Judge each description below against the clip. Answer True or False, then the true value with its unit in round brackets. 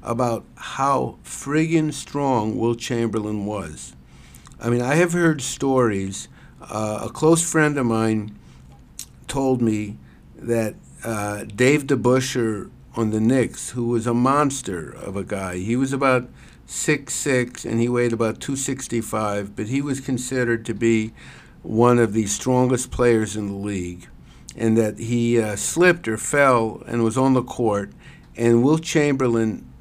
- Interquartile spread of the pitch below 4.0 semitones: True (3.6 semitones)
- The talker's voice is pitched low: True (115 Hz)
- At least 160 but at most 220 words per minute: False (145 wpm)